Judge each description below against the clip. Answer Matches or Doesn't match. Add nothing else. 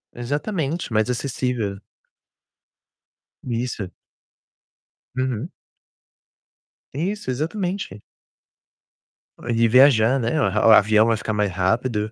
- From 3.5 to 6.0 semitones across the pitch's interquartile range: Matches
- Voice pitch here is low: Matches